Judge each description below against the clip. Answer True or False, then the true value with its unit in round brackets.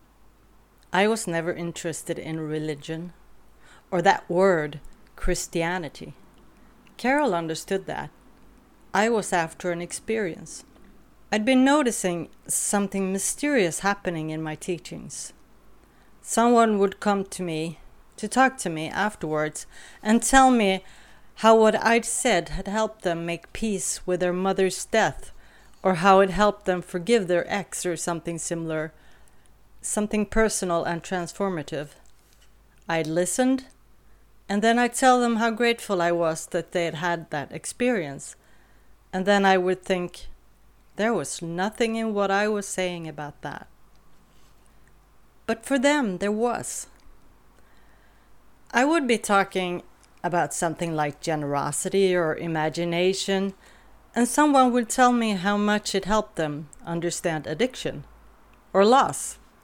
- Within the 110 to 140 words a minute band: True (130 wpm)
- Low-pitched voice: False (190 Hz)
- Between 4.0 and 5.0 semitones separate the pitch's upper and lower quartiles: True (4.4 semitones)